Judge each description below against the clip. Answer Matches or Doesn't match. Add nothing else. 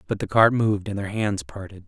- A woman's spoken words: Doesn't match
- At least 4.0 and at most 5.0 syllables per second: Doesn't match